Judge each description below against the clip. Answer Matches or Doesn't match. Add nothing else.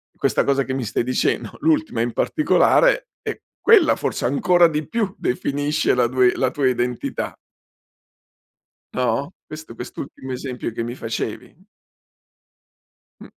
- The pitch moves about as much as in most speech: Doesn't match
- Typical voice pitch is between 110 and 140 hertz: Matches